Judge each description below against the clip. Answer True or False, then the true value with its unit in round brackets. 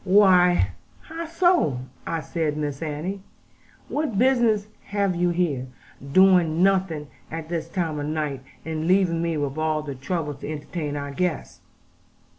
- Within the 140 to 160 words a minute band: True (145 wpm)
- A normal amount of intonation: True (4.2 semitones)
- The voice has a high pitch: False (165 Hz)